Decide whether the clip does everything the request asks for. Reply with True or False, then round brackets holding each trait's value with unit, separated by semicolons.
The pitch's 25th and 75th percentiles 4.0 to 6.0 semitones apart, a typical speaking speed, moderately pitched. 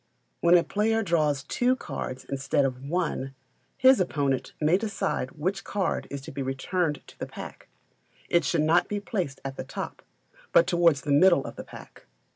True (5.2 semitones; 180 wpm; 155 Hz)